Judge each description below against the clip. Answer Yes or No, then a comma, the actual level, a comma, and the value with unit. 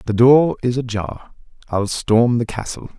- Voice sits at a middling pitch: No, low, 115 Hz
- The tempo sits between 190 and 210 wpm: No, average, 160 wpm